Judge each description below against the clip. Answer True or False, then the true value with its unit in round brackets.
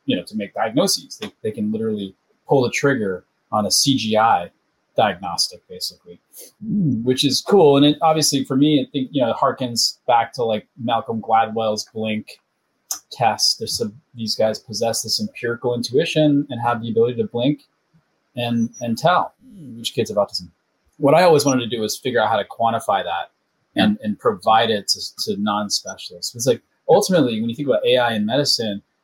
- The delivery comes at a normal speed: True (185 wpm)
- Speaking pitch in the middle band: False (120 Hz)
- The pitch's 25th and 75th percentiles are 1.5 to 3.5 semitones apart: False (4.5 semitones)